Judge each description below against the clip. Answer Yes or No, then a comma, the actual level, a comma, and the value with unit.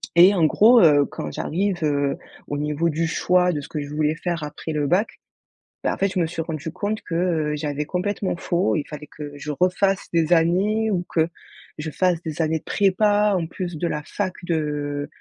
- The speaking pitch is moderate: Yes, medium, 165 Hz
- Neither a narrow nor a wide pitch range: Yes, average, 3.5 semitones